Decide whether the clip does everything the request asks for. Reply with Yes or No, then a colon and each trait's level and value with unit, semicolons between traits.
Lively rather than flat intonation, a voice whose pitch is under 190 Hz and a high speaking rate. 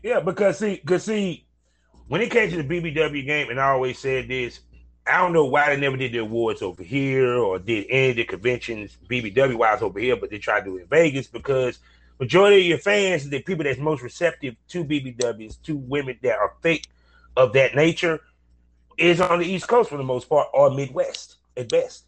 Yes: wide, 6.4 semitones; low, 135 Hz; fast, 215 wpm